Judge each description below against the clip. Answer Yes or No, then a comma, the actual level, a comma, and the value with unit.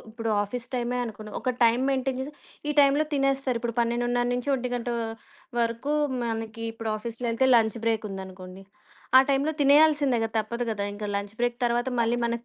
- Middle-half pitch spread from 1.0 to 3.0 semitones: Yes, narrow, 2.5 semitones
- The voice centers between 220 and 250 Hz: Yes, high, 235 Hz